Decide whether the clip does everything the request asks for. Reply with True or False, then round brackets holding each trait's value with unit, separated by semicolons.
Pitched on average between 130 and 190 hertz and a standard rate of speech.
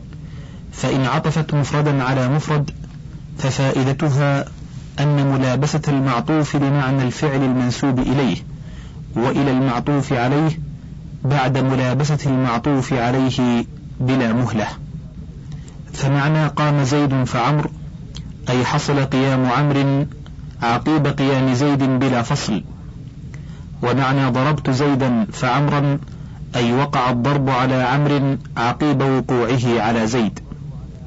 True (140 Hz; 95 wpm)